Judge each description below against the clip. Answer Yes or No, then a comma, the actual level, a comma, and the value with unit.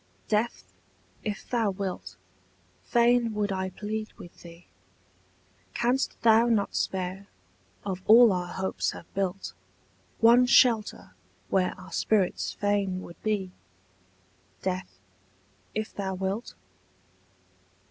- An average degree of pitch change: Yes, average, 3.0 semitones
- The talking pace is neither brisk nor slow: No, slow, 105 wpm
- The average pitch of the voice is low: No, high, 200 Hz